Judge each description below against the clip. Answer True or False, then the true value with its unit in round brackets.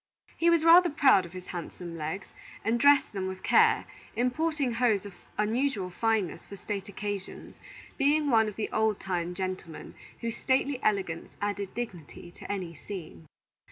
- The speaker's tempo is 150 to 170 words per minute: True (155 wpm)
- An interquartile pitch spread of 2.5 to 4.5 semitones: False (5.2 semitones)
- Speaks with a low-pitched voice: False (205 Hz)